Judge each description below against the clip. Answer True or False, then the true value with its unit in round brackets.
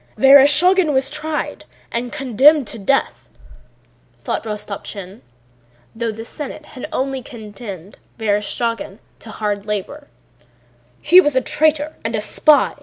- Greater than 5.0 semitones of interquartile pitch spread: True (5.6 semitones)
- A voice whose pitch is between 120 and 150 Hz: False (250 Hz)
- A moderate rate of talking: False (120 wpm)